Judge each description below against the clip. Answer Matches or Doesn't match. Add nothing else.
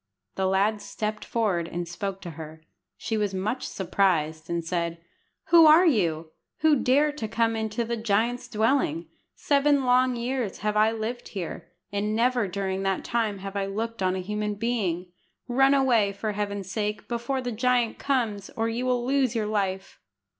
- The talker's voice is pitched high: Matches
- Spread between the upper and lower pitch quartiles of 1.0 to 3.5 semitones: Doesn't match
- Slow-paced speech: Doesn't match